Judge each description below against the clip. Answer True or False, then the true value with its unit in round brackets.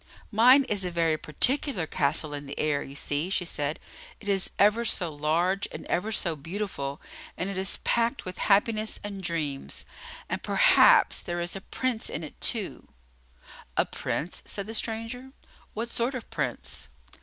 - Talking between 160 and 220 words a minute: True (165 wpm)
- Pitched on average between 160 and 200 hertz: True (190 Hz)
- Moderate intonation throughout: False (6.1 semitones)